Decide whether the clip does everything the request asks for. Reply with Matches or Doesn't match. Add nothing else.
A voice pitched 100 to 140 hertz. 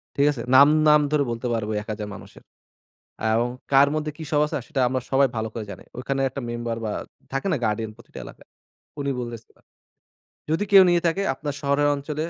Matches